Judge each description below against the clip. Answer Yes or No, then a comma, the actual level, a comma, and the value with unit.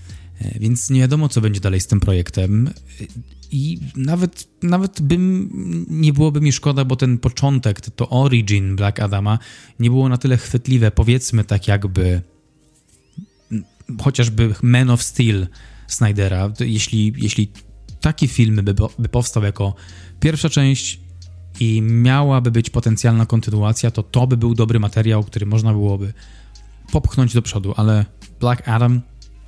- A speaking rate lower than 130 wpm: No, average, 135 wpm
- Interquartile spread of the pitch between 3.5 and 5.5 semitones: Yes, average, 3.8 semitones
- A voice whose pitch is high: No, low, 115 Hz